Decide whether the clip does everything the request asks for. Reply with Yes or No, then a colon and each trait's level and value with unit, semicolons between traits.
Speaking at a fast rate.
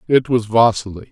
No: average, 160 wpm